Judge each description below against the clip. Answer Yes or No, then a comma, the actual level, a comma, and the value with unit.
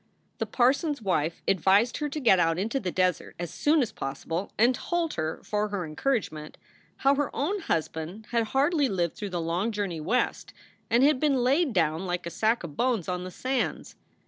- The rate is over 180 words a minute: Yes, average, 200 wpm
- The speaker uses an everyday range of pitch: No, wide, 7.5 semitones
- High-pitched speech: Yes, high, 210 Hz